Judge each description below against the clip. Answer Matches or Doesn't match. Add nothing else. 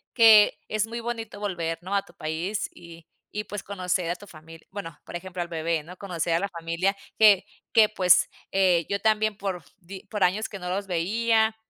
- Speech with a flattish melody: Doesn't match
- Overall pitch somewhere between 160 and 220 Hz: Matches